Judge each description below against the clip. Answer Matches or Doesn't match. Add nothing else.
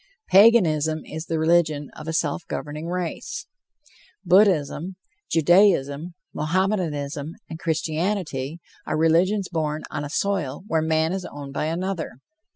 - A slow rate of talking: Matches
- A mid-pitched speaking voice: Matches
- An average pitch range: Matches